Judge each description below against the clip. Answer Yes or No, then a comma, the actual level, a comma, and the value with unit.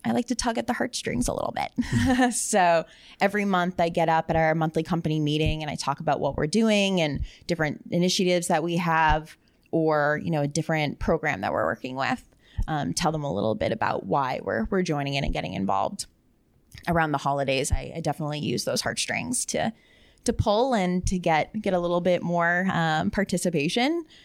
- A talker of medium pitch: Yes, medium, 170 Hz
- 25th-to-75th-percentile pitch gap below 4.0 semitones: Yes, average, 3.4 semitones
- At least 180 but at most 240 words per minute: Yes, average, 200 wpm